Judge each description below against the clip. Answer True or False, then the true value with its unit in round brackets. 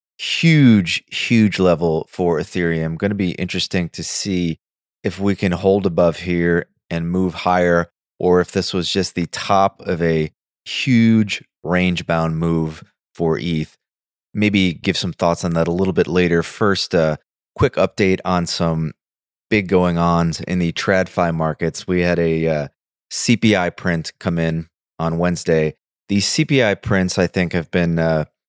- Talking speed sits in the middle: True (160 wpm)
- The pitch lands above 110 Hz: False (90 Hz)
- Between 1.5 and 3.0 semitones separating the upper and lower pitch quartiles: True (2.5 semitones)